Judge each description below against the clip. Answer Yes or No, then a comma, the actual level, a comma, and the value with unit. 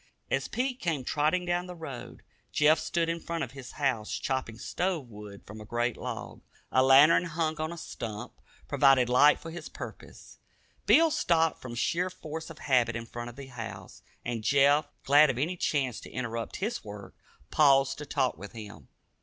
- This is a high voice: No, medium, 140 Hz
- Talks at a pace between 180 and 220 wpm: Yes, average, 185 wpm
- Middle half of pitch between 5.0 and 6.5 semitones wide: Yes, wide, 5.5 semitones